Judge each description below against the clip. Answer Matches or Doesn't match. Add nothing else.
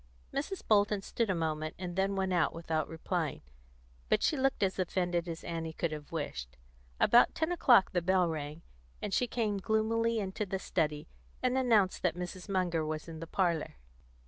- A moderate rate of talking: Matches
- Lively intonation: Doesn't match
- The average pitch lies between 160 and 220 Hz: Matches